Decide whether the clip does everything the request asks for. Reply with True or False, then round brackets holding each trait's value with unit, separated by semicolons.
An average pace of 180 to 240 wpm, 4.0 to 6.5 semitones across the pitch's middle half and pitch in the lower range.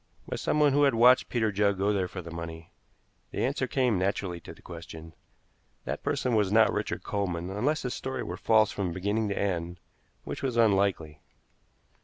True (185 wpm; 5.0 semitones; 100 Hz)